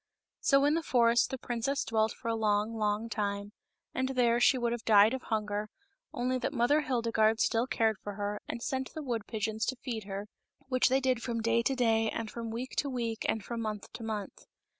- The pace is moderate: No, fast, 215 wpm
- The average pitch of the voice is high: Yes, high, 230 Hz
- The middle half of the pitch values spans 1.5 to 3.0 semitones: Yes, average, 2.7 semitones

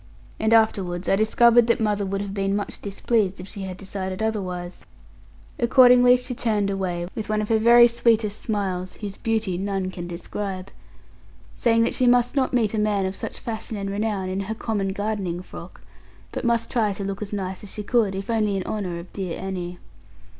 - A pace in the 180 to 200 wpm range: Yes, average, 195 wpm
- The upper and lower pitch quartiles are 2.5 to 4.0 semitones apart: Yes, average, 2.8 semitones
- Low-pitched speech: No, high, 205 Hz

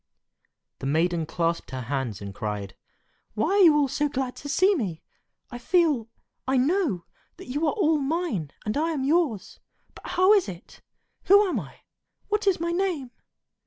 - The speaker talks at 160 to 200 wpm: Yes, average, 165 wpm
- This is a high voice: Yes, very high, 275 Hz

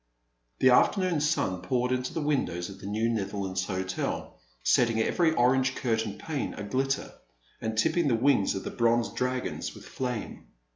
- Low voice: Yes, low, 120 Hz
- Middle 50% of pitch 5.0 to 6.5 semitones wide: No, average, 4.5 semitones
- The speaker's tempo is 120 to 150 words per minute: No, average, 160 wpm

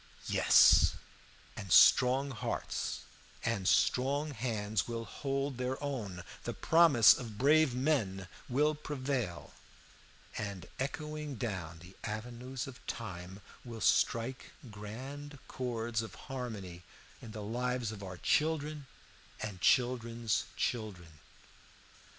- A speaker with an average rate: No, slow, 110 wpm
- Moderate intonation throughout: Yes, average, 4.5 semitones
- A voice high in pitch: No, low, 120 Hz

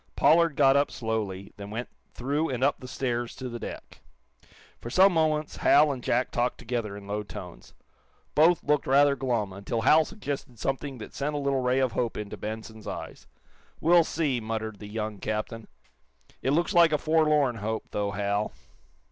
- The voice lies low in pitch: Yes, low, 125 Hz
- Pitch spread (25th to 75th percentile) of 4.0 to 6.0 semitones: Yes, average, 5.0 semitones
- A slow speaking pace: No, average, 180 wpm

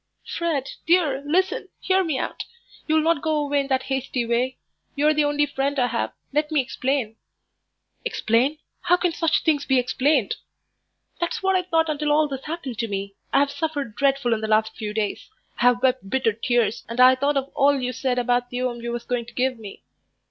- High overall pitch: Yes, very high, 270 Hz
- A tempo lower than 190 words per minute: No, fast, 205 wpm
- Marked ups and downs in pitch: No, average, 3.8 semitones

